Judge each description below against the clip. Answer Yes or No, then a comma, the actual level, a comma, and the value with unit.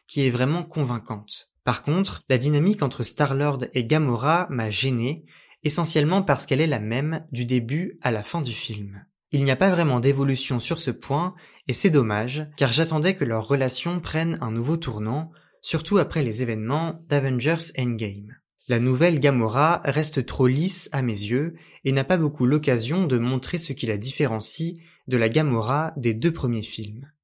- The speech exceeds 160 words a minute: Yes, average, 180 wpm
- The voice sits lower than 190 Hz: Yes, medium, 140 Hz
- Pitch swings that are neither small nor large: Yes, average, 4.5 semitones